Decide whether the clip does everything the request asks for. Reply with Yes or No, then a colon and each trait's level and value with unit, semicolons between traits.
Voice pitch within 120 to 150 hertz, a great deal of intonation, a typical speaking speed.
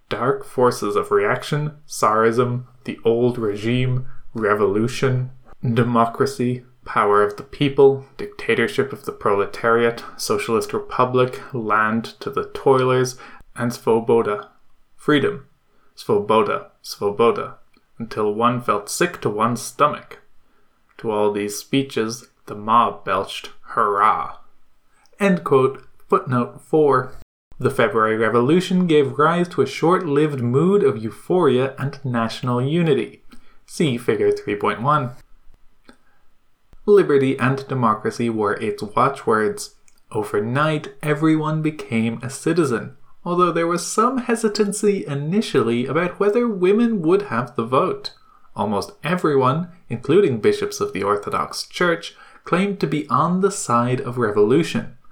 No: low, 135 Hz; wide, 7.4 semitones; slow, 115 wpm